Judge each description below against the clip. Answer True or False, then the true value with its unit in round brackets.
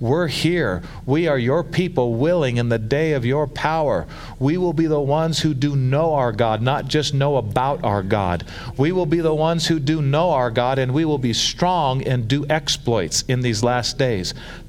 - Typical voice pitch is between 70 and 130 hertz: False (140 Hz)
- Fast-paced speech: True (210 wpm)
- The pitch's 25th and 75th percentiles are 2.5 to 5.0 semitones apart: True (4.3 semitones)